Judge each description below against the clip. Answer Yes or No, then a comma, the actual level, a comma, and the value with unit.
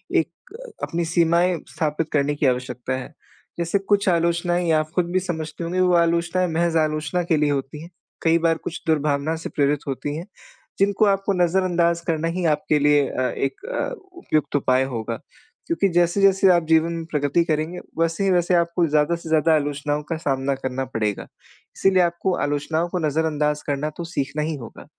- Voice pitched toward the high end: No, medium, 160 Hz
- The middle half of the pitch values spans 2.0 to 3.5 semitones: Yes, average, 2.7 semitones